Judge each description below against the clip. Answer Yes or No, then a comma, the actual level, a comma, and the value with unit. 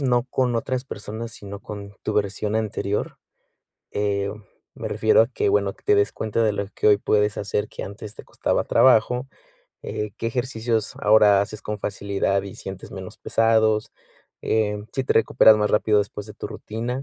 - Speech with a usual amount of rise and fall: No, narrow, 2.1 semitones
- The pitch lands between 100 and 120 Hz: Yes, low, 105 Hz